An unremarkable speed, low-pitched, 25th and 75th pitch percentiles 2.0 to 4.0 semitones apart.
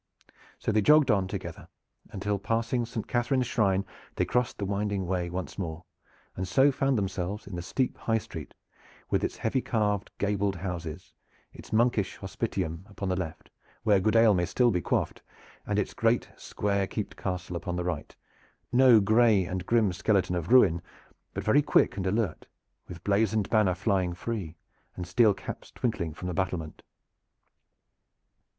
Yes: average, 165 wpm; low, 100 Hz; average, 3.7 semitones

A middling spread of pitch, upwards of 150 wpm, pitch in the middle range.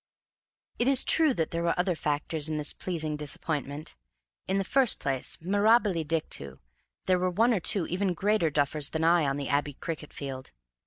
Yes: average, 4.4 semitones; average, 180 wpm; medium, 165 Hz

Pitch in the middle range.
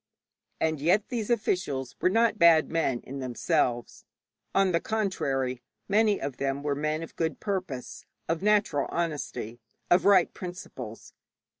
Yes: medium, 165 Hz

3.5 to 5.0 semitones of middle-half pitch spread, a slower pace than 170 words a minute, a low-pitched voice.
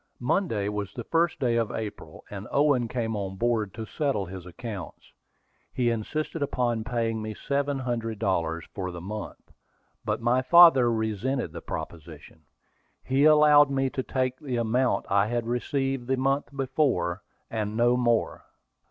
Yes: average, 4.2 semitones; average, 155 wpm; low, 120 Hz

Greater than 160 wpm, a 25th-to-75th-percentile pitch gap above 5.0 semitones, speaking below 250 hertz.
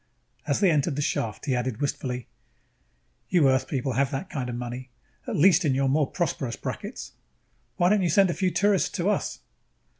Yes: average, 190 wpm; wide, 5.5 semitones; medium, 140 Hz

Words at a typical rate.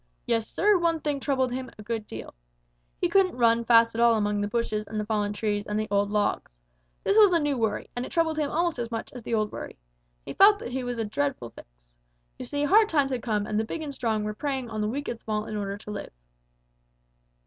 No: fast, 250 wpm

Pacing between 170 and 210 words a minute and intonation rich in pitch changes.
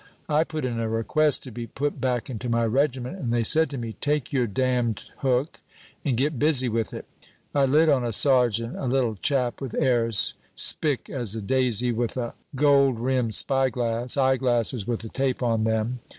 No: average, 195 wpm; average, 2.8 semitones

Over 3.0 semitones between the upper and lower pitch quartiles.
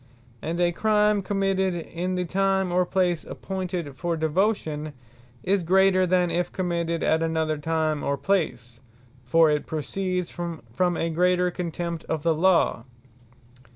No: average, 2.7 semitones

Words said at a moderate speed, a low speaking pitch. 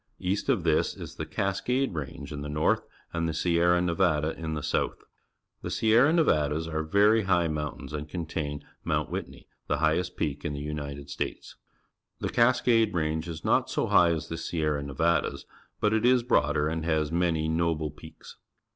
Yes: average, 180 wpm; very low, 80 Hz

